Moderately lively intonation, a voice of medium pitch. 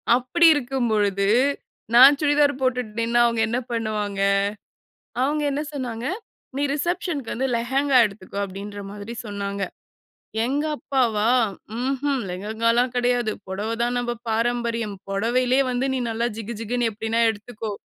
No: average, 3.4 semitones; high, 235 Hz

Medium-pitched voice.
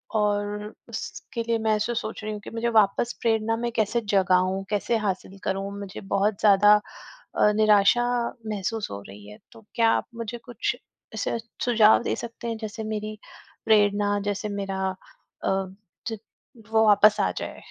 No: high, 210 Hz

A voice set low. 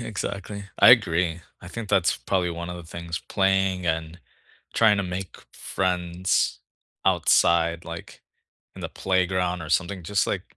Yes: very low, 90 Hz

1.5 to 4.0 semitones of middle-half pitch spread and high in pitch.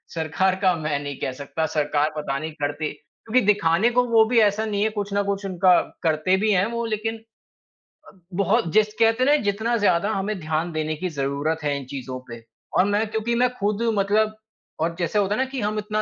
No: wide, 5.4 semitones; high, 195 Hz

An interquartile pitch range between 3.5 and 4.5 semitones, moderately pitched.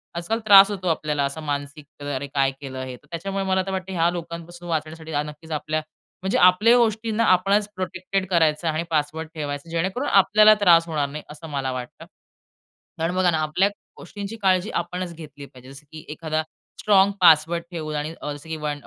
Yes: average, 3.9 semitones; medium, 165 Hz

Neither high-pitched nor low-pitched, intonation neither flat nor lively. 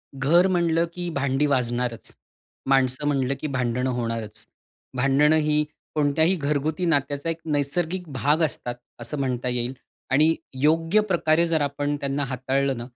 Yes: medium, 145 Hz; average, 3.5 semitones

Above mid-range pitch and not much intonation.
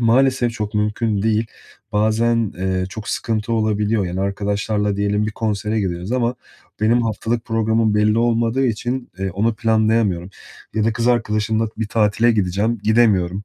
No: low, 110 Hz; narrow, 1.9 semitones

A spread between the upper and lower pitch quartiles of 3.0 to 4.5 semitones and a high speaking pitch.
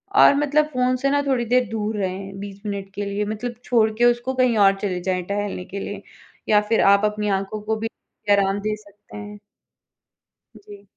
Yes: average, 3.3 semitones; high, 210 Hz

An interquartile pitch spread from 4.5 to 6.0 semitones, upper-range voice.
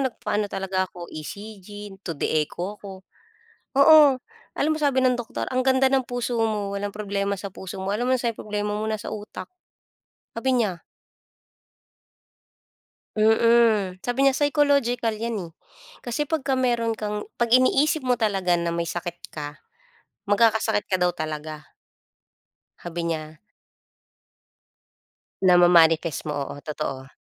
Yes: wide, 5.4 semitones; high, 210 Hz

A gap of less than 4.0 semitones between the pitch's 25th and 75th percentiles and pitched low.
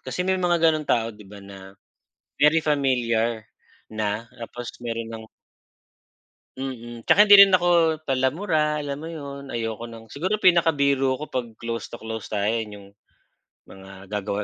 No: wide, 5.5 semitones; low, 120 Hz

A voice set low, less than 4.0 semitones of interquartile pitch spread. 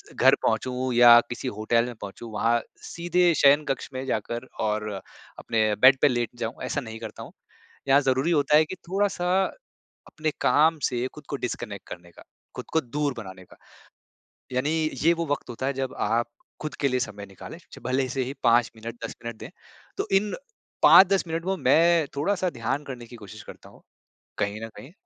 No: low, 130 Hz; average, 4.6 semitones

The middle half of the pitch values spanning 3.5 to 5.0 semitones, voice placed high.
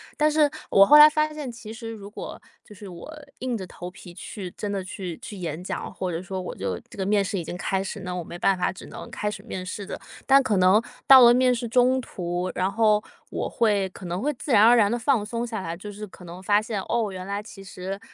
Yes: average, 4.1 semitones; high, 205 Hz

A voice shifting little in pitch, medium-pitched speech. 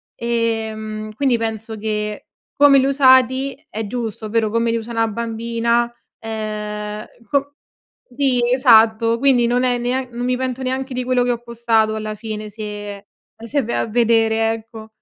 No: narrow, 2.3 semitones; high, 230 Hz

